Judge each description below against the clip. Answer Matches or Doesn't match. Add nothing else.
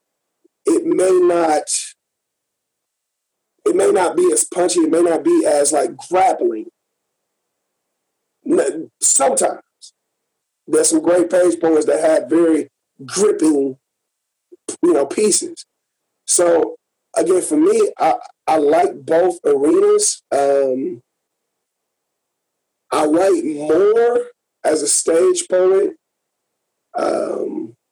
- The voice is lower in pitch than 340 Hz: Doesn't match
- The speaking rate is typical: Doesn't match